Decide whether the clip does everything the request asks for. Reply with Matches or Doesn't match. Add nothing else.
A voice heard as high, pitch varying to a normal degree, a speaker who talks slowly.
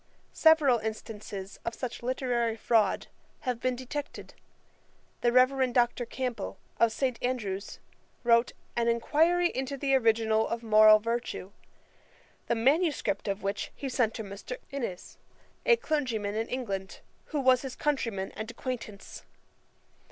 Matches